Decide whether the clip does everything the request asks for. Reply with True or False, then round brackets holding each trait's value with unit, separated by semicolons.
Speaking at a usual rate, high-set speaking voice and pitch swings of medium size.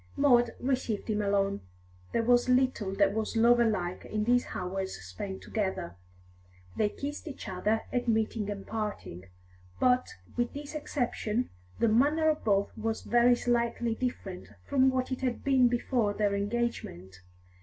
True (150 wpm; 225 Hz; 3.7 semitones)